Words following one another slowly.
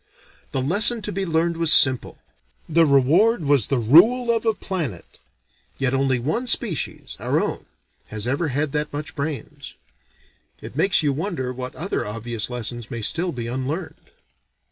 No: average, 160 wpm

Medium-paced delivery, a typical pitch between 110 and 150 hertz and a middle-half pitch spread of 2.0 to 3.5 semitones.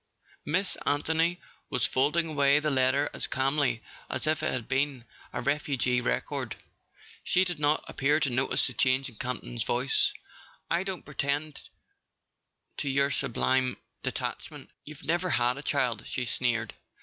Yes: average, 150 wpm; medium, 140 Hz; average, 3.0 semitones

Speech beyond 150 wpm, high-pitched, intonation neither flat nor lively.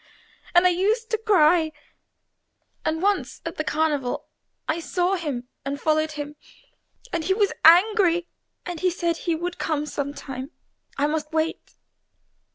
No: average, 145 wpm; very high, 325 Hz; average, 3.1 semitones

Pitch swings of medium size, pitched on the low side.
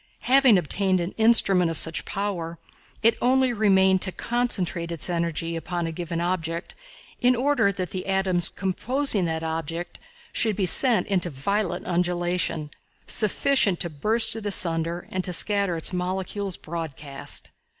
No: average, 3.6 semitones; medium, 185 Hz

